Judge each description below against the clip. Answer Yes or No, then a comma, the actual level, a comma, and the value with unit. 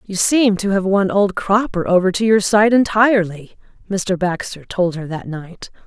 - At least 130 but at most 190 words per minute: Yes, average, 185 wpm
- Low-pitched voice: No, high, 195 Hz